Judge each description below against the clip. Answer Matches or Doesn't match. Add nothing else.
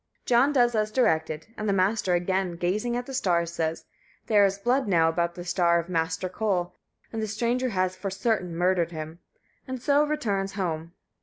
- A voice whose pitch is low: Doesn't match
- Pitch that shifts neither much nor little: Matches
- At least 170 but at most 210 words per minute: Matches